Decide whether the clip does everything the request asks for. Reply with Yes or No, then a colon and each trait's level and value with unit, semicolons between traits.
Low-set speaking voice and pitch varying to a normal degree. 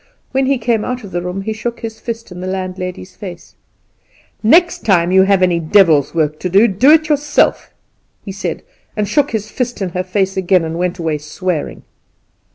No: high, 190 Hz; average, 4.1 semitones